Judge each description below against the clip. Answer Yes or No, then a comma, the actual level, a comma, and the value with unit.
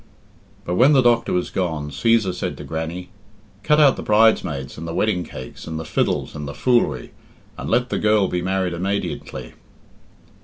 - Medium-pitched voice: No, very low, 90 Hz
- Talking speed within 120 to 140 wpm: No, average, 180 wpm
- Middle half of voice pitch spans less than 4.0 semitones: No, wide, 5.6 semitones